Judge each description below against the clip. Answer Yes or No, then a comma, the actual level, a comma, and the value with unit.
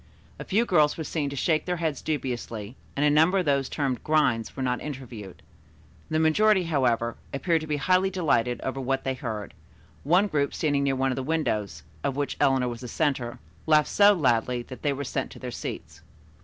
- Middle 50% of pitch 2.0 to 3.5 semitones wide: No, average, 4.0 semitones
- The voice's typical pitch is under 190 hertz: Yes, medium, 140 Hz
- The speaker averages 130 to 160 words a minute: No, fast, 205 wpm